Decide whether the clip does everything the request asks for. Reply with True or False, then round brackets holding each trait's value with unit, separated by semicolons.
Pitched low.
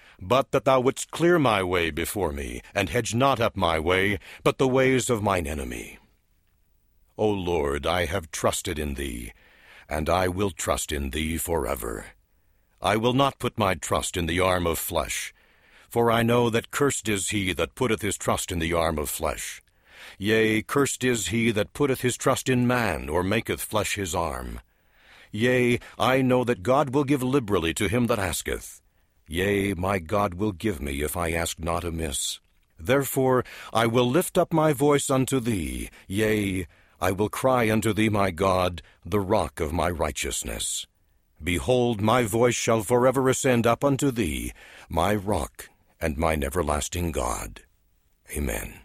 True (100 Hz)